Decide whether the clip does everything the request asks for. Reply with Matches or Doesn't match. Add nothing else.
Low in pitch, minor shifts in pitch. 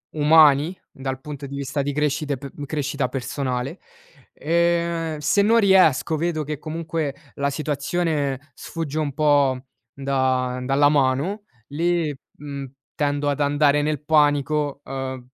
Doesn't match